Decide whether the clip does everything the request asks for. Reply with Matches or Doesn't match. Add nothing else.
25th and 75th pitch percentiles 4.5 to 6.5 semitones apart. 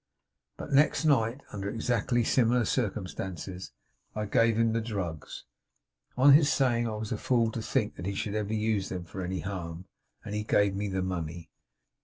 Doesn't match